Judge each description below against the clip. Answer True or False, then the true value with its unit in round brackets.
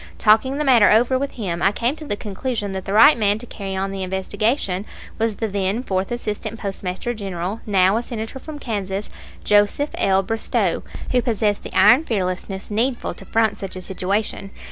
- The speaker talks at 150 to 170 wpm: False (190 wpm)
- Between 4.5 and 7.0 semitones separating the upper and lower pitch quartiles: False (3.4 semitones)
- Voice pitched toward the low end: False (210 Hz)